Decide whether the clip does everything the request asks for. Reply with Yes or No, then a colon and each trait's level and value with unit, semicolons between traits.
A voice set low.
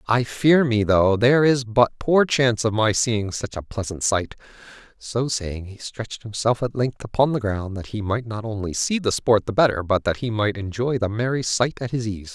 Yes: low, 115 Hz